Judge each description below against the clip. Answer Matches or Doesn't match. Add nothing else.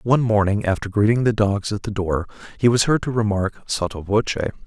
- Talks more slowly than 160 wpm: Doesn't match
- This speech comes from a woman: Doesn't match